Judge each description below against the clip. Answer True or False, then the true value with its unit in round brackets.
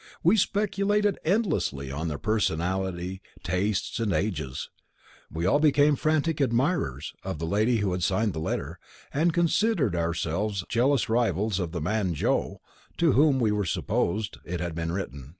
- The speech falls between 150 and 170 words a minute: True (155 wpm)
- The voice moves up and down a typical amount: False (9.0 semitones)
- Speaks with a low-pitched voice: True (105 Hz)